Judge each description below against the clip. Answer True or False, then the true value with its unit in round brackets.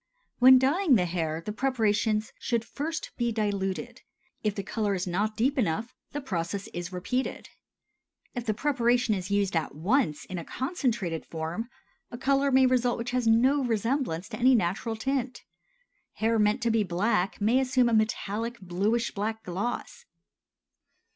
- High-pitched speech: True (225 Hz)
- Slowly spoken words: False (160 wpm)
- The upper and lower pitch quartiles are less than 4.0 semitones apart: False (4.5 semitones)